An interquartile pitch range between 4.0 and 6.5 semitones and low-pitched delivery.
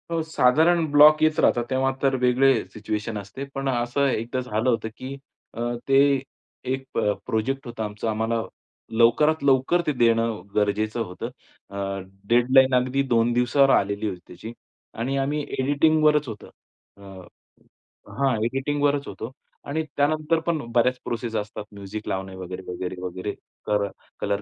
Yes: average, 4.3 semitones; low, 125 Hz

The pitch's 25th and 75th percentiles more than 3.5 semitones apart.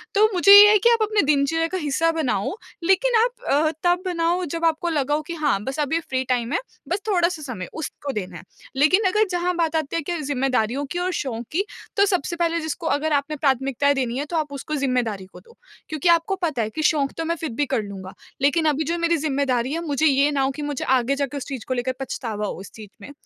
Yes: average, 4.2 semitones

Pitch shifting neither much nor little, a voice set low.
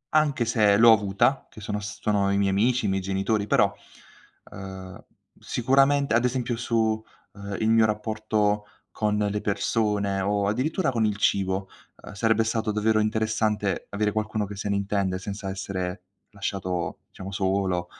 No: narrow, 2.0 semitones; low, 105 Hz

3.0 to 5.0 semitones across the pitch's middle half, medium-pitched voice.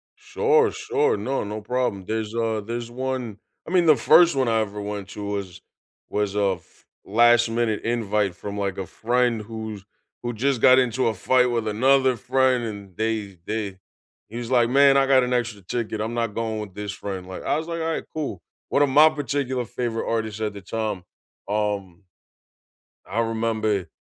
No: average, 3.7 semitones; low, 115 Hz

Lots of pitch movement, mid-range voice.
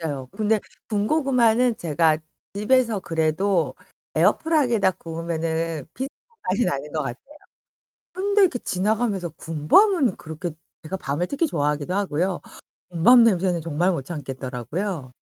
Yes: wide, 6.4 semitones; medium, 180 Hz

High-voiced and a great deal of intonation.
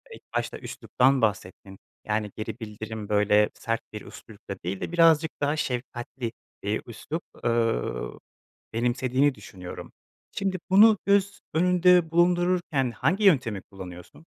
No: low, 125 Hz; wide, 8.2 semitones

